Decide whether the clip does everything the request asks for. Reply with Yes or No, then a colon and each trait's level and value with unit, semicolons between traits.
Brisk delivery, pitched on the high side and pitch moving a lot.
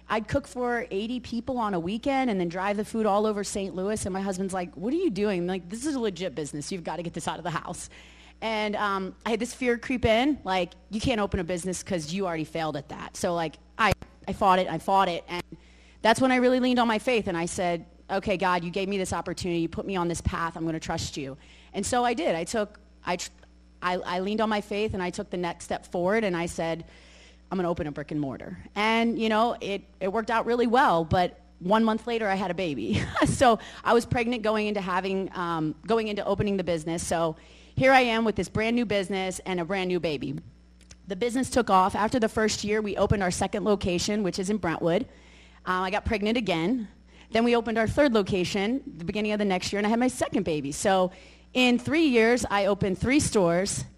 No: fast, 250 wpm; high, 195 Hz; average, 4.1 semitones